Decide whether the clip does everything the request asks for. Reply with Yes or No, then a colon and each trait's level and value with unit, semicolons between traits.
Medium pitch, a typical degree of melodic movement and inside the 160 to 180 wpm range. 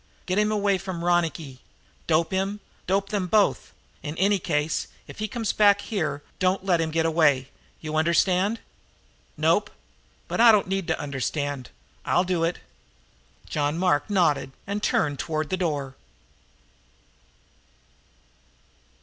No: medium, 175 Hz; average, 4.3 semitones; slow, 135 wpm